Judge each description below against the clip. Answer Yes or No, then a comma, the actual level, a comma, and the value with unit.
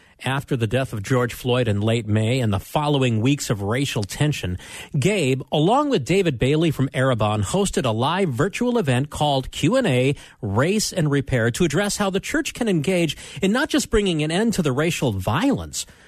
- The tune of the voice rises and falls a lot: Yes, wide, 7.4 semitones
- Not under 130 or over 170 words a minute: No, average, 185 wpm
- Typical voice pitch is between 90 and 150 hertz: Yes, medium, 140 Hz